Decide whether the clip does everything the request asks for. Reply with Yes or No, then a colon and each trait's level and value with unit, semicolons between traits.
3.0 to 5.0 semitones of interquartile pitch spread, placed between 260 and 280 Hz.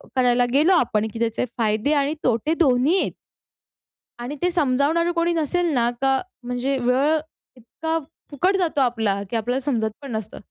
Yes: average, 4.7 semitones; very high, 265 Hz